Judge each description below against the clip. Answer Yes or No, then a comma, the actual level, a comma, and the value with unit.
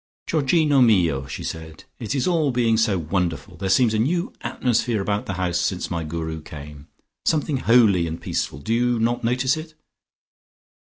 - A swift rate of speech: No, average, 170 wpm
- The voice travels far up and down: Yes, wide, 7.1 semitones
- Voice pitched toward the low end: Yes, low, 110 Hz